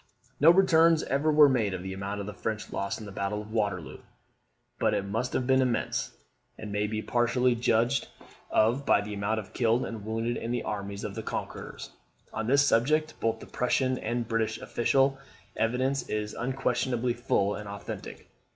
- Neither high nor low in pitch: No, low, 115 Hz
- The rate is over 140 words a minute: Yes, average, 185 wpm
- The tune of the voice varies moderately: Yes, average, 3.5 semitones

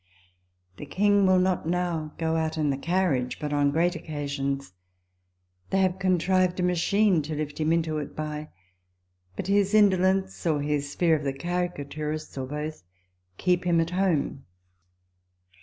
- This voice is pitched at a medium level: Yes, medium, 165 Hz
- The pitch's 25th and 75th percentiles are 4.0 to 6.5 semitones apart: No, average, 3.6 semitones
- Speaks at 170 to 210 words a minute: No, average, 155 wpm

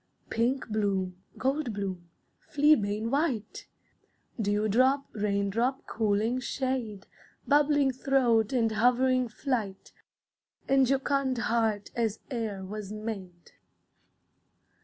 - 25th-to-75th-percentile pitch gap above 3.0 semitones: Yes, average, 4.2 semitones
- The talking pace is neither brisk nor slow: No, slow, 90 wpm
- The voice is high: Yes, high, 230 Hz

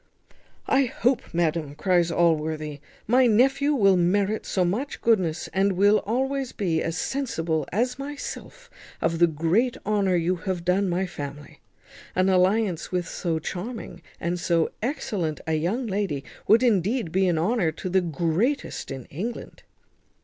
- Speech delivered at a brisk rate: No, average, 150 wpm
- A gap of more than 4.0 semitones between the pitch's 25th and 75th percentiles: Yes, wide, 5.5 semitones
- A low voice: No, medium, 185 Hz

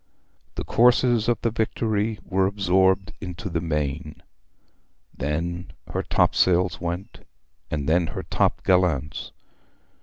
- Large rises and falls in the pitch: No, average, 3.8 semitones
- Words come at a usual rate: No, slow, 115 wpm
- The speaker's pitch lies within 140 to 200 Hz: No, very low, 90 Hz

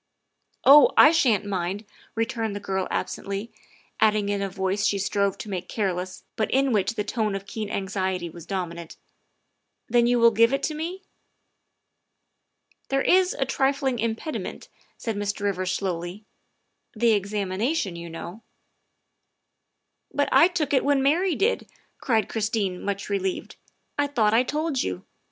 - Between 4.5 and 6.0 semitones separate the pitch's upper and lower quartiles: Yes, average, 5.2 semitones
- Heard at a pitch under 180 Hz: No, high, 210 Hz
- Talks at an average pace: Yes, average, 165 wpm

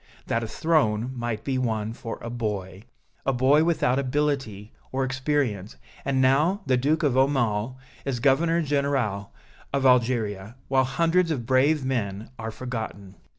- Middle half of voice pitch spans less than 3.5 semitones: No, average, 3.9 semitones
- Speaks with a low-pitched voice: Yes, low, 130 Hz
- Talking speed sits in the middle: Yes, average, 150 wpm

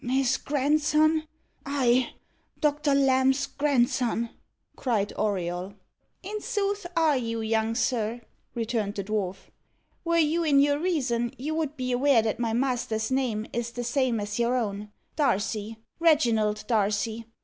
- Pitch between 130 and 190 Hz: No, high, 245 Hz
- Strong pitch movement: No, average, 4.7 semitones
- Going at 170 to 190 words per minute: No, slow, 135 wpm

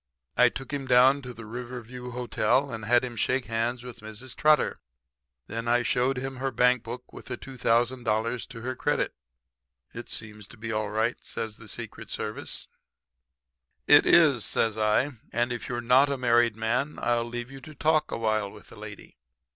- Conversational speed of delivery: Yes, average, 185 wpm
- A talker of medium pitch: No, low, 120 Hz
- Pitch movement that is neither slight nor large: No, narrow, 2.1 semitones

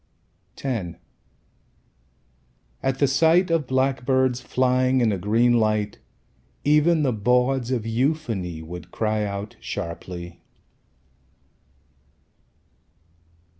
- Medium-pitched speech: No, low, 125 Hz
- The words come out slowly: Yes, slow, 90 wpm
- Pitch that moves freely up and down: No, average, 4.3 semitones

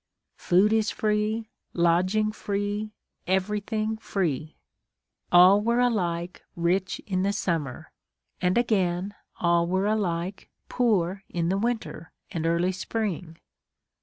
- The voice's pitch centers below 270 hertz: Yes, high, 190 Hz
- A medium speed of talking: No, slow, 110 wpm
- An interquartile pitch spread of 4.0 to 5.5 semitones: No, average, 3.6 semitones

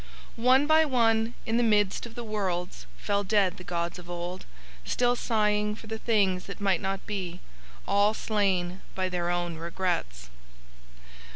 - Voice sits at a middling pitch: No, high, 200 Hz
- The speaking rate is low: No, average, 160 wpm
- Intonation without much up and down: No, average, 3.8 semitones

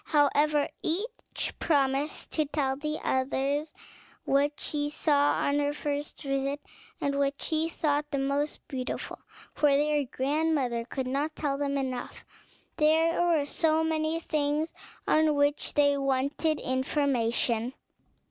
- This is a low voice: No, very high, 290 Hz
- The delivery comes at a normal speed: No, slow, 130 wpm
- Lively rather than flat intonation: No, narrow, 1.9 semitones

